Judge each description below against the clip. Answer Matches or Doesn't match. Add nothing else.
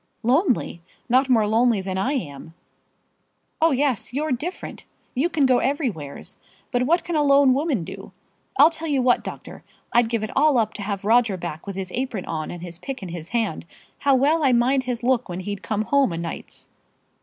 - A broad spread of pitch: Matches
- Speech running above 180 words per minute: Matches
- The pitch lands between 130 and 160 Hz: Doesn't match